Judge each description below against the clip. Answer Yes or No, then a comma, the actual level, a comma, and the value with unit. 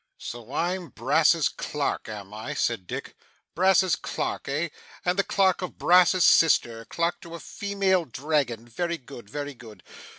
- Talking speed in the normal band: Yes, average, 155 wpm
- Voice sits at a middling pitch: Yes, medium, 155 Hz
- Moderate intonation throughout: No, wide, 7.0 semitones